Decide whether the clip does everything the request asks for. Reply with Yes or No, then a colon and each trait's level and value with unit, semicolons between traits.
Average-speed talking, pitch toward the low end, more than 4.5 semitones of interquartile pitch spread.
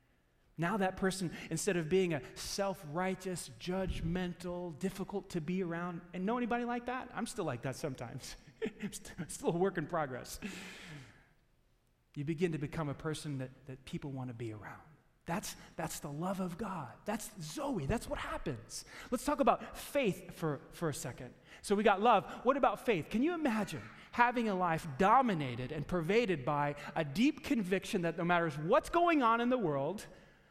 No: average, 180 wpm; medium, 180 Hz; average, 5.2 semitones